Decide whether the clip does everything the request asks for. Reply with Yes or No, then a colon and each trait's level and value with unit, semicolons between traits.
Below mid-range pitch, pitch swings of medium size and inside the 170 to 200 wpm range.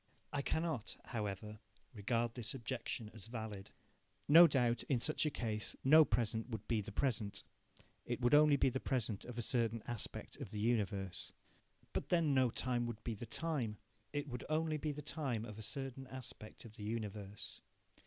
Yes: low, 120 Hz; average, 3.9 semitones; average, 180 wpm